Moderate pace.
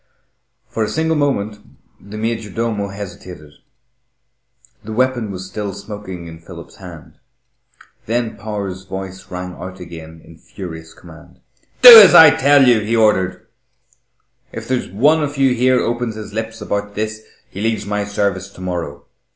Yes: average, 150 wpm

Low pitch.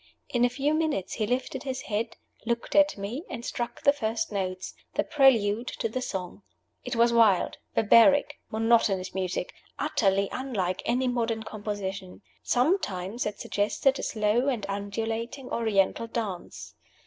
No: high, 225 Hz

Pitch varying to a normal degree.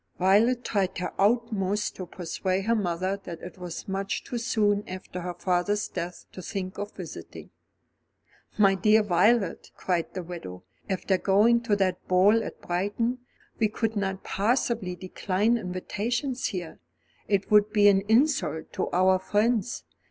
Yes: average, 3.1 semitones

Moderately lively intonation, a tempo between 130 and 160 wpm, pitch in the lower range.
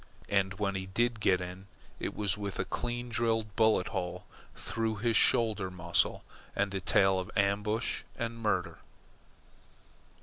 Yes: average, 3.0 semitones; average, 145 wpm; low, 100 Hz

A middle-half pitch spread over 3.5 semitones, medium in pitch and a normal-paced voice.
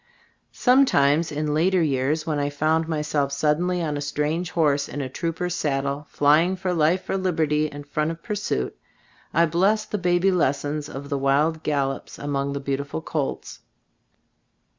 No: average, 3.0 semitones; medium, 150 Hz; average, 160 wpm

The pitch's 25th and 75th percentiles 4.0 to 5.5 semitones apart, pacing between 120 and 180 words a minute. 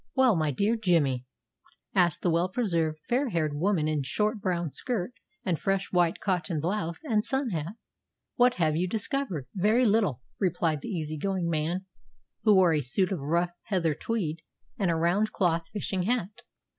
Yes: average, 4.5 semitones; average, 170 wpm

